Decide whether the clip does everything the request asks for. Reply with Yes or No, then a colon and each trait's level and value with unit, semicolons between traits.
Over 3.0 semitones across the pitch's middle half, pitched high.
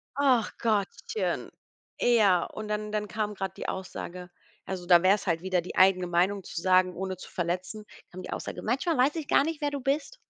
Yes: average, 4.4 semitones; high, 195 Hz